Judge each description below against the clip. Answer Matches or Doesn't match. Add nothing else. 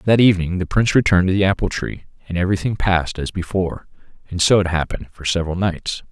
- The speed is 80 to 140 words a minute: Doesn't match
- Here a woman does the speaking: Doesn't match